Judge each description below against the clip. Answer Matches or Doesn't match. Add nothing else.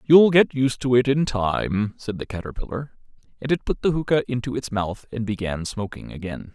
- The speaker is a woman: Doesn't match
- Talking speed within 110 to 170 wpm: Doesn't match